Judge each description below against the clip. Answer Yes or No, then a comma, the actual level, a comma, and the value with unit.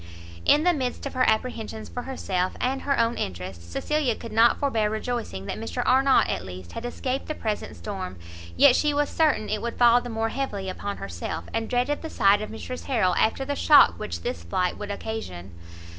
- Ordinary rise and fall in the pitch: Yes, average, 5.0 semitones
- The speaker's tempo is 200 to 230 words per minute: Yes, fast, 205 wpm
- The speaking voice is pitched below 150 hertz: No, high, 225 Hz